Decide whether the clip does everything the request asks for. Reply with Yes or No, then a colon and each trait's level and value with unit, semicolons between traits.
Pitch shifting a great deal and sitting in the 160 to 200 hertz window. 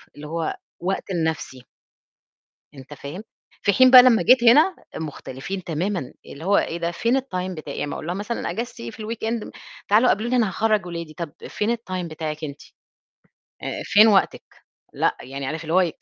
Yes: wide, 6.0 semitones; medium, 185 Hz